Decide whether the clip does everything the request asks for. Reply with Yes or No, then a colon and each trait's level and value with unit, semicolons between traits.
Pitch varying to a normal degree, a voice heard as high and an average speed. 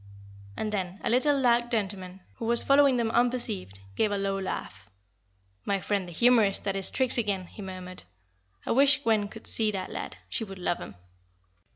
Yes: average, 4.1 semitones; high, 205 Hz; average, 185 wpm